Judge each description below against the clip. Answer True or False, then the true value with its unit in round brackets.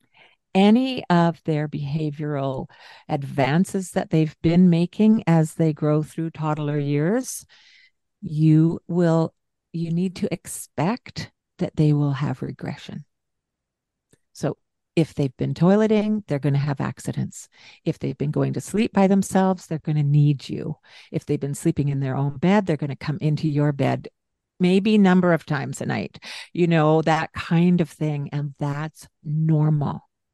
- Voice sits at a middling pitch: True (155 Hz)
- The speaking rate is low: False (155 wpm)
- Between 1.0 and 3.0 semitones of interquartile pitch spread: False (3.4 semitones)